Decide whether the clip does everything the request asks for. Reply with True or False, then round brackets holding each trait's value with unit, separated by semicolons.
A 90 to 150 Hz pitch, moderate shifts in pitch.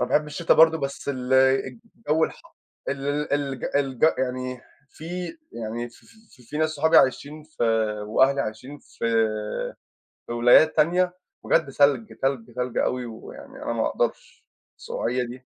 True (135 Hz; 3.2 semitones)